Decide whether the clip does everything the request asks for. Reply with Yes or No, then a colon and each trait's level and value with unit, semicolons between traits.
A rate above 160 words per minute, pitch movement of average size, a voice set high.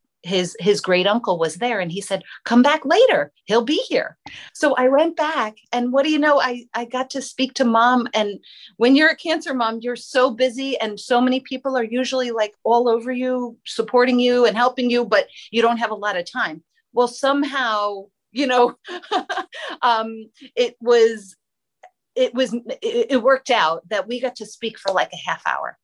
Yes: average, 200 wpm; average, 3.0 semitones; high, 245 Hz